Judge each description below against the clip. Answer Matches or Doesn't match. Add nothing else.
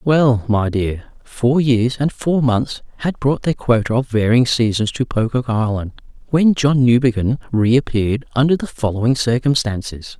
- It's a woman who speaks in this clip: Doesn't match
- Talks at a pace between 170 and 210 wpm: Doesn't match